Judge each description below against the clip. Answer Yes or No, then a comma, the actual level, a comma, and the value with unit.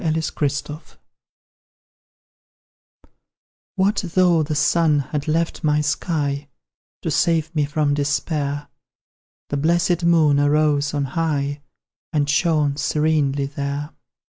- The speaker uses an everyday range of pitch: No, narrow, 2.1 semitones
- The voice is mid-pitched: Yes, medium, 150 Hz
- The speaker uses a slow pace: Yes, slow, 100 wpm